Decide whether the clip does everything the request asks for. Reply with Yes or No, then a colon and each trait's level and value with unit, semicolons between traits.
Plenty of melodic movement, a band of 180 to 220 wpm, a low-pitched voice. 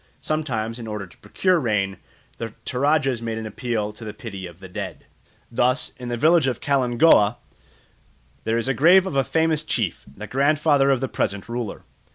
No: average, 4.8 semitones; average, 185 wpm; low, 120 Hz